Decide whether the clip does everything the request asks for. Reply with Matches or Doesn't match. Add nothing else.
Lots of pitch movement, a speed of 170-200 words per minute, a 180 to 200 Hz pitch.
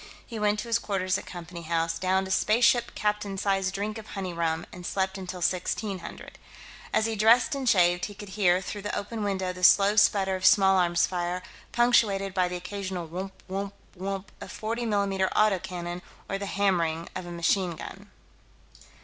Doesn't match